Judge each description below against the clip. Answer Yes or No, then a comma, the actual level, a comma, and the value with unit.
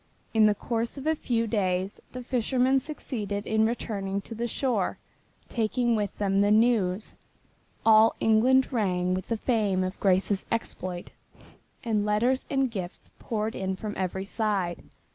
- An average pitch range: Yes, average, 3.4 semitones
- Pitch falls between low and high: No, high, 215 Hz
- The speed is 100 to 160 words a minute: Yes, average, 150 wpm